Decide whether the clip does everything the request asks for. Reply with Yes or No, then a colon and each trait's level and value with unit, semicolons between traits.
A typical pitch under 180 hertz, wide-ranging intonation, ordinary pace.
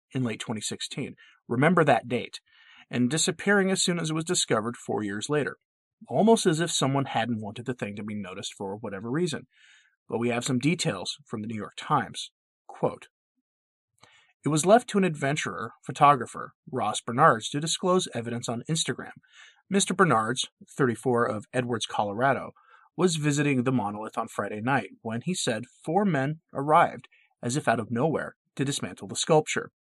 Yes: low, 135 Hz; wide, 6.1 semitones; average, 170 wpm